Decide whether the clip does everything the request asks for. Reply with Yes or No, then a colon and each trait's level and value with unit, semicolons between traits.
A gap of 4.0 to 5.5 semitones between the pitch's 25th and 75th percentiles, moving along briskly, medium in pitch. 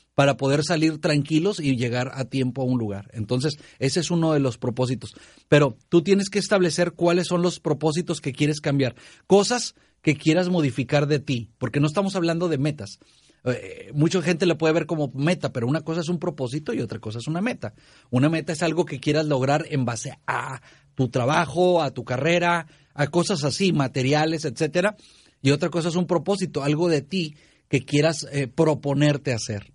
Yes: average, 4.3 semitones; fast, 195 wpm; medium, 150 Hz